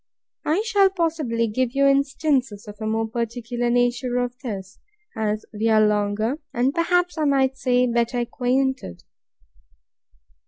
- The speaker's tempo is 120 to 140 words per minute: Yes, slow, 135 wpm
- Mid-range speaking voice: No, high, 245 Hz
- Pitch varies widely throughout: No, average, 3.7 semitones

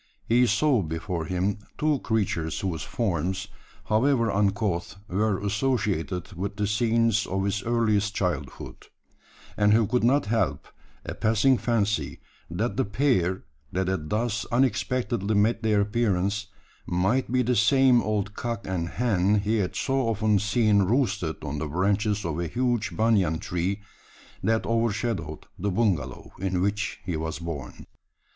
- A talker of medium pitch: No, low, 105 Hz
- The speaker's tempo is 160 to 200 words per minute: No, average, 145 wpm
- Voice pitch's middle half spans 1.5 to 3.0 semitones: No, average, 3.8 semitones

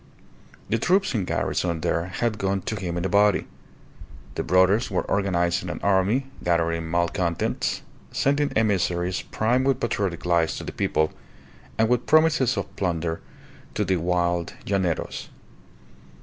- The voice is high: No, very low, 95 Hz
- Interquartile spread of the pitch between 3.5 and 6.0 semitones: Yes, average, 4.2 semitones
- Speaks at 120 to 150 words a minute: Yes, average, 140 wpm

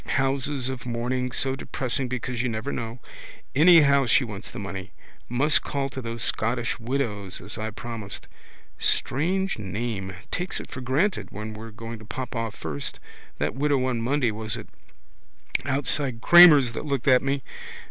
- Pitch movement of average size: Yes, average, 3.5 semitones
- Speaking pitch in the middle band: No, low, 125 Hz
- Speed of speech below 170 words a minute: Yes, average, 155 wpm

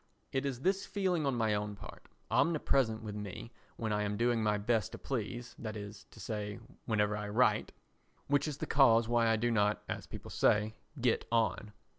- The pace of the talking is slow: No, average, 185 wpm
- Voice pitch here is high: No, low, 115 Hz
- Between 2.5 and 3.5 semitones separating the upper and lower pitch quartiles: Yes, average, 3.0 semitones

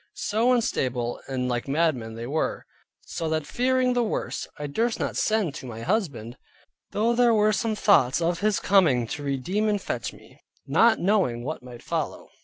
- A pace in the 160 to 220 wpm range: Yes, average, 180 wpm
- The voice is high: No, medium, 170 Hz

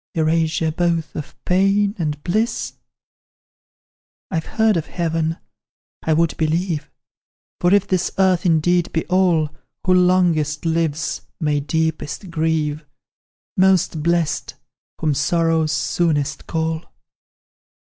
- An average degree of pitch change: No, narrow, 2.3 semitones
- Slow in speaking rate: Yes, slow, 105 wpm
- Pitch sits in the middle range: Yes, medium, 165 Hz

